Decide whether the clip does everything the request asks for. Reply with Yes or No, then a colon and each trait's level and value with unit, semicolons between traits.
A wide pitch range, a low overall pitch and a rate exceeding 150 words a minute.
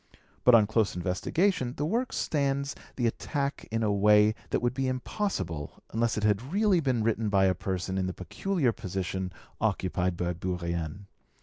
Yes: wide, 6.6 semitones; low, 110 Hz; average, 170 wpm